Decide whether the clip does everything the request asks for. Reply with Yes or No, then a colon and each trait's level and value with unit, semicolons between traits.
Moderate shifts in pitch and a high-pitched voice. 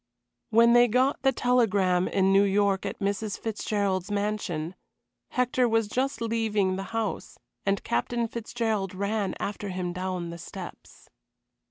Yes: average, 3.2 semitones; high, 205 Hz